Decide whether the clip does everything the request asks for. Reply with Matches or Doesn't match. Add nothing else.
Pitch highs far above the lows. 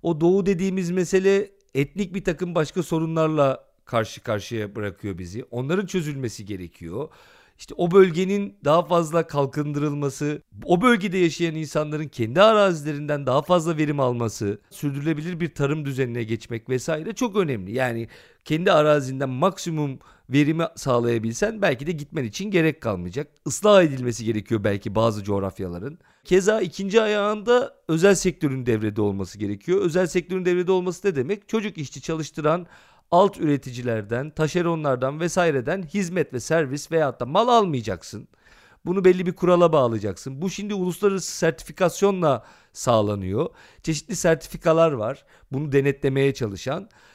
Matches